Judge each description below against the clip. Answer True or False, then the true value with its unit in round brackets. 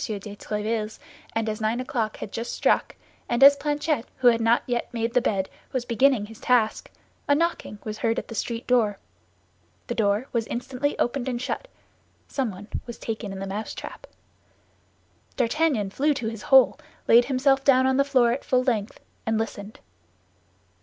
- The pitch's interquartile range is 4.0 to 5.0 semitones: False (3.3 semitones)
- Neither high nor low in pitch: False (235 Hz)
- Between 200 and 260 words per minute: False (170 wpm)